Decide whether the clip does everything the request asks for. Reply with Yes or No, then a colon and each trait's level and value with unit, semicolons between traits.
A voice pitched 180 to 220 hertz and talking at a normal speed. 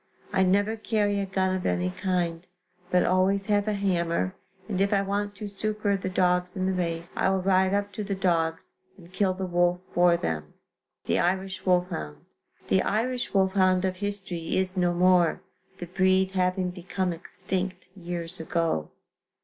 Yes: medium, 185 Hz; average, 170 wpm